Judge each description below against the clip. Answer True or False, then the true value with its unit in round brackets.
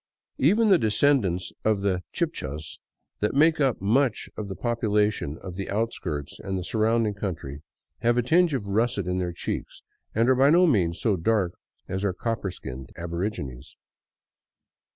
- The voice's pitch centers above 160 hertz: False (105 Hz)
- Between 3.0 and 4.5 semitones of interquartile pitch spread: False (5.0 semitones)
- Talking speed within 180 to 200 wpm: False (160 wpm)